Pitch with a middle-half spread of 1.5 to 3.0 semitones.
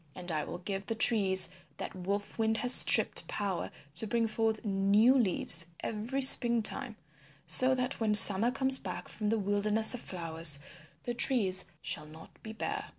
No: average, 3.7 semitones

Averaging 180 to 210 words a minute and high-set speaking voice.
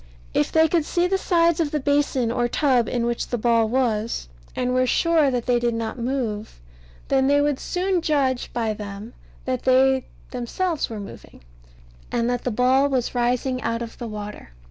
Yes: average, 190 wpm; very high, 250 Hz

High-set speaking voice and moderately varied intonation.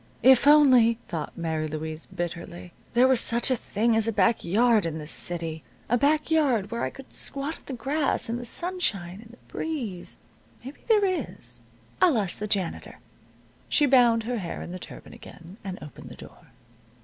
No: high, 230 Hz; wide, 7.0 semitones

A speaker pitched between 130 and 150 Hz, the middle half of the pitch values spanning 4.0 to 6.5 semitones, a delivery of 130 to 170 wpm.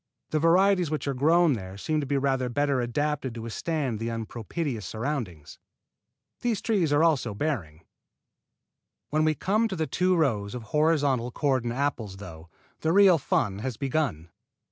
Yes: medium, 140 Hz; wide, 5.6 semitones; average, 160 wpm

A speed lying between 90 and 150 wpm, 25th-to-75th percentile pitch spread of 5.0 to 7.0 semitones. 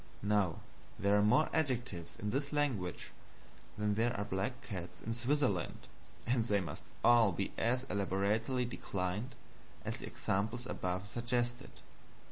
No: slow, 135 wpm; average, 3.7 semitones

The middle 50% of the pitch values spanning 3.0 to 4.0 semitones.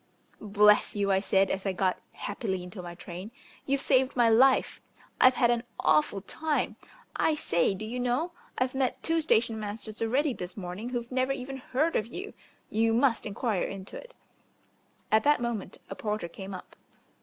No: average, 4.7 semitones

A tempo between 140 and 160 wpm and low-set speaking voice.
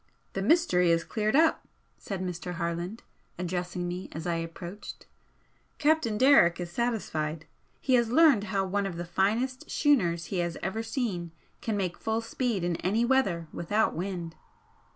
No: average, 155 wpm; high, 190 Hz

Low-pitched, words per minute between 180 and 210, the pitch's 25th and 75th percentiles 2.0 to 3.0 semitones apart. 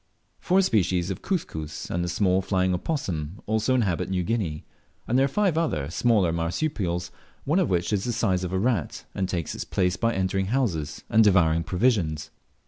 No: very low, 95 Hz; average, 185 wpm; average, 5.2 semitones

